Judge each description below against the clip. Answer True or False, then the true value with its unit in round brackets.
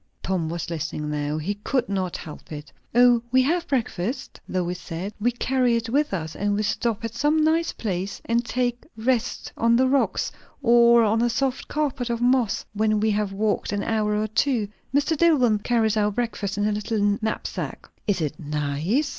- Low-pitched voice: False (220 Hz)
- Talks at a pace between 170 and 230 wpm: True (190 wpm)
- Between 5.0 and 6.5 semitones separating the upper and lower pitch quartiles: False (3.8 semitones)